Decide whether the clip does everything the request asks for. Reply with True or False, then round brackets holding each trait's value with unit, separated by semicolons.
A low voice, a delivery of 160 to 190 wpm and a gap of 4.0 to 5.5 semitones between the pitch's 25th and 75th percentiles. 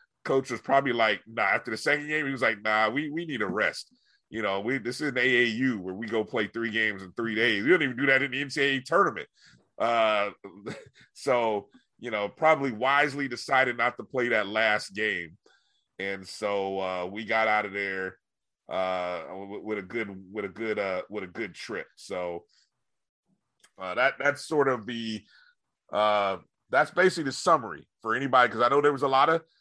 False (115 Hz; 200 wpm; 4.9 semitones)